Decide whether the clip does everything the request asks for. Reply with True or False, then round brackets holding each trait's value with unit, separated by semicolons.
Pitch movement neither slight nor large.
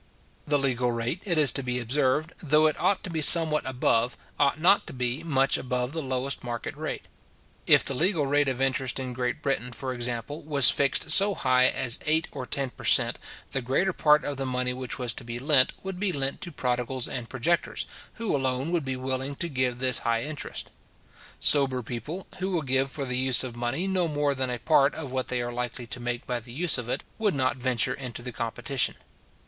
True (3.2 semitones)